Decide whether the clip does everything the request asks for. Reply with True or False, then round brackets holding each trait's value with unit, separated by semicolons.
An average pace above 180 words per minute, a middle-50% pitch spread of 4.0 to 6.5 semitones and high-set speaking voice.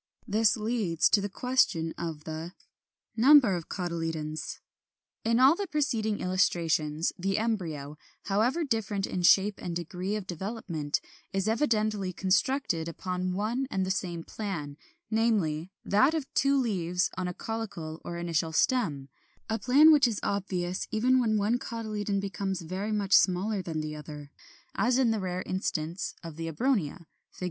False (155 wpm; 4.9 semitones; 195 Hz)